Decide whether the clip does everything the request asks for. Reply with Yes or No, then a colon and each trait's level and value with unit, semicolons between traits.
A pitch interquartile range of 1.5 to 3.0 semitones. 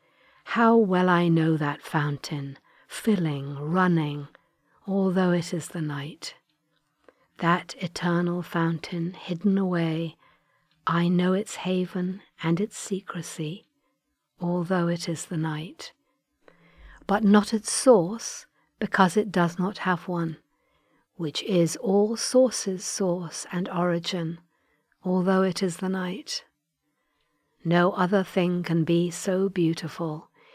Yes: narrow, 2.6 semitones